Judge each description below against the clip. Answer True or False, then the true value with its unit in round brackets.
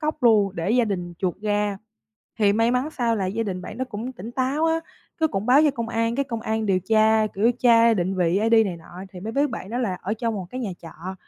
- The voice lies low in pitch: False (220 Hz)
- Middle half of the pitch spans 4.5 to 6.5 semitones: False (3.8 semitones)